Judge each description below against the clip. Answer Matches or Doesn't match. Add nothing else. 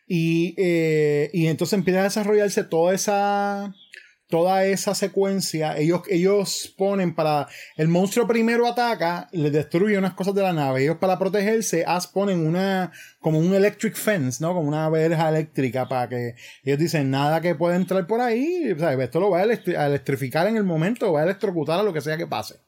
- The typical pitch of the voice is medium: Matches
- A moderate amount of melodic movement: Matches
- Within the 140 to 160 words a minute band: Doesn't match